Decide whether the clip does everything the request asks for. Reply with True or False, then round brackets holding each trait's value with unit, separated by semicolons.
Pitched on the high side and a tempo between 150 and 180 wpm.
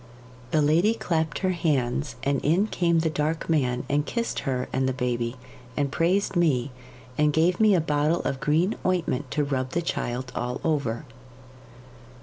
False (150 Hz; 165 wpm)